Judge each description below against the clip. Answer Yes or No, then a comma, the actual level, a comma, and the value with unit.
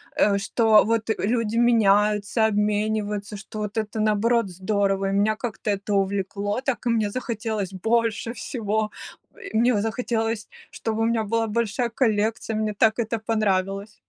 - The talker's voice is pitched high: Yes, high, 215 Hz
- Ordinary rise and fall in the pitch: No, narrow, 1.9 semitones